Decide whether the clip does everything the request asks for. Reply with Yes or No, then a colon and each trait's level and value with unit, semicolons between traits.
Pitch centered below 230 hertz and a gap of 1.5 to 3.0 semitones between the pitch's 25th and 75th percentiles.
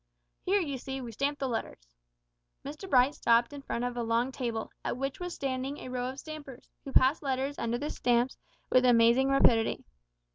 No: very high, 260 Hz; narrow, 2.6 semitones